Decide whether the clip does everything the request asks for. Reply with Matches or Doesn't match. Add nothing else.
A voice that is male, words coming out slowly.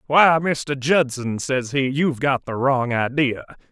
Doesn't match